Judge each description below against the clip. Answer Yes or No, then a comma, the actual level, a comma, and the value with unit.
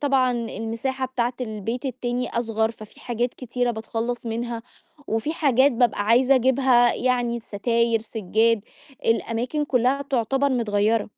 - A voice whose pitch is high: Yes, high, 240 Hz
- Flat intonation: Yes, narrow, 2.1 semitones